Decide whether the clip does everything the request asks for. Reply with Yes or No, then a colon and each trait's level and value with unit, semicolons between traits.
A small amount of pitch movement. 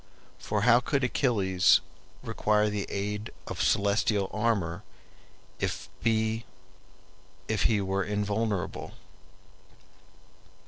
Yes: narrow, 2.2 semitones